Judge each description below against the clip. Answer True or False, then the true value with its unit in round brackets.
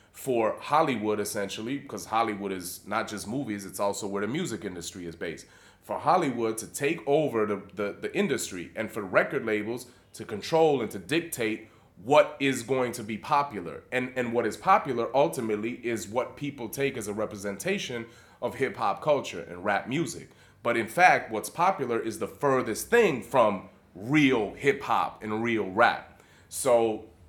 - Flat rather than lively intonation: False (3.9 semitones)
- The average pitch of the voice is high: False (115 Hz)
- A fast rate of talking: False (170 wpm)